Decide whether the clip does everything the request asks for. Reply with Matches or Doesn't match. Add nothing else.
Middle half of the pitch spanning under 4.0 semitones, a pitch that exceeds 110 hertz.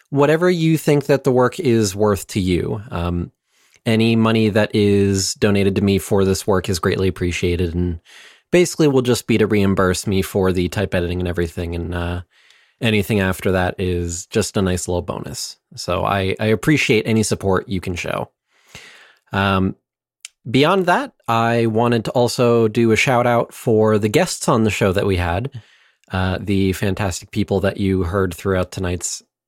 Doesn't match